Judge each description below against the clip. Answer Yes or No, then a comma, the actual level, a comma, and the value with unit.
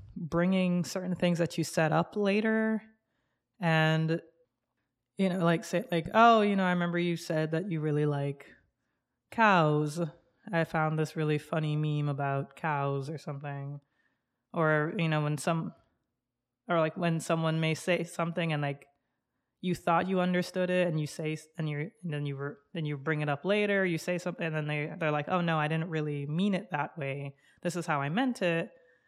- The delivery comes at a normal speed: Yes, average, 190 wpm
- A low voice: No, medium, 160 Hz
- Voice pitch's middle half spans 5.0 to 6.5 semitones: No, average, 2.9 semitones